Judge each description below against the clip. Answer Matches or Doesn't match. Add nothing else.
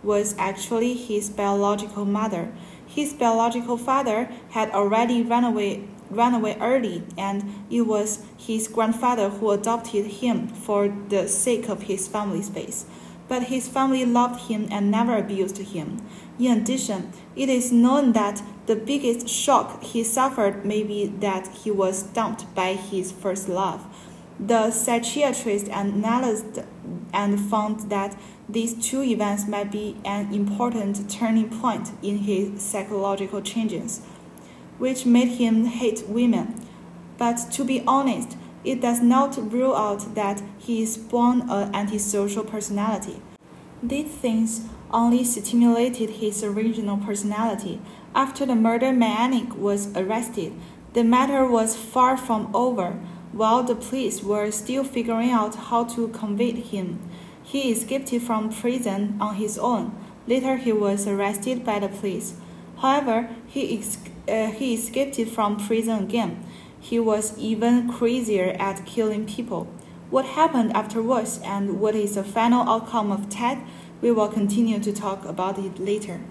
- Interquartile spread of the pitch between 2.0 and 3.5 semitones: Matches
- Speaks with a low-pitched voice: Doesn't match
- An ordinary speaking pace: Matches